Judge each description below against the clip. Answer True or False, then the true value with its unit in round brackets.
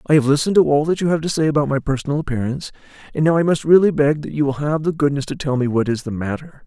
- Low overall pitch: False (145 Hz)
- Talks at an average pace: False (295 wpm)